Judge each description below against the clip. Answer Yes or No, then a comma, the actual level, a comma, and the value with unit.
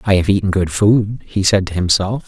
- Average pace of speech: No, fast, 235 wpm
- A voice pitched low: Yes, low, 100 Hz